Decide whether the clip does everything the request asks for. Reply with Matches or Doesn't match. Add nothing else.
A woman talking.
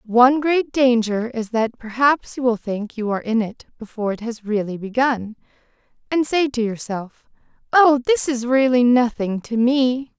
Matches